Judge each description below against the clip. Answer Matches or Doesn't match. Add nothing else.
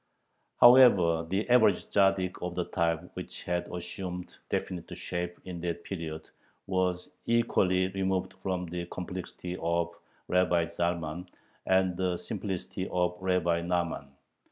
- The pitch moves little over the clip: Matches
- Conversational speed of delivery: Doesn't match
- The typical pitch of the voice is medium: Doesn't match